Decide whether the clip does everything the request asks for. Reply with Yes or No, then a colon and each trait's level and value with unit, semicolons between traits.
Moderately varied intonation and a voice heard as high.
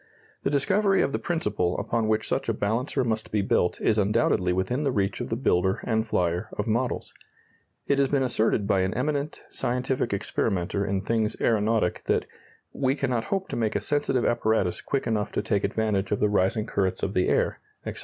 No: average, 4.3 semitones; low, 110 Hz